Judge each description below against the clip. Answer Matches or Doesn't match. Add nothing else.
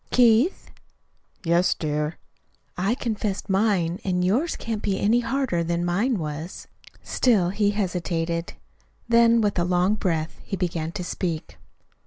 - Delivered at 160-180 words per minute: Doesn't match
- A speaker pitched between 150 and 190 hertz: Matches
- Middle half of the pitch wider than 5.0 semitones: Doesn't match